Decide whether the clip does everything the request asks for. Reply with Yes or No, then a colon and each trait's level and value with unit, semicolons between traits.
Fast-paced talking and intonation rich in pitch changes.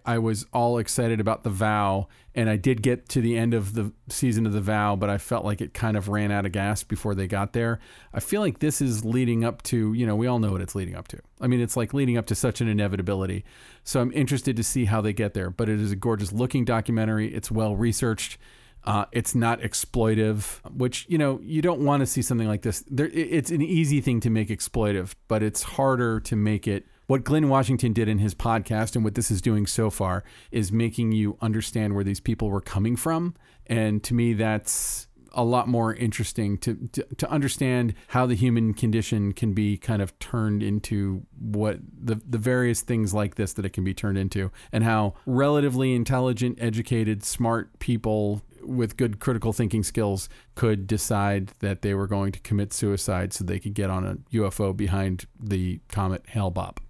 No: fast, 215 wpm; average, 2.9 semitones